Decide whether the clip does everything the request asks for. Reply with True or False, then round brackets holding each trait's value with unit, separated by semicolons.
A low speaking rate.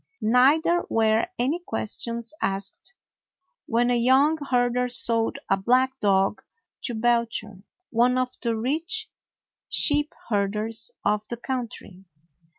True (115 wpm)